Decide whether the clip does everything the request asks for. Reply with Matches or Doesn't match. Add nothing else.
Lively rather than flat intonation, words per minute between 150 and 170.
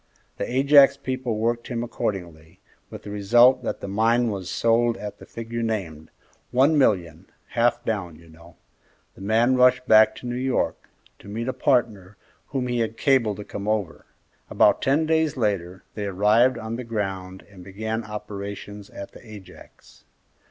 Doesn't match